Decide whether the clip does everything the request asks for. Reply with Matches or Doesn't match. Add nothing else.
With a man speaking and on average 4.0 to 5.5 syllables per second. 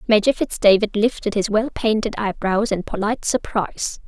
Doesn't match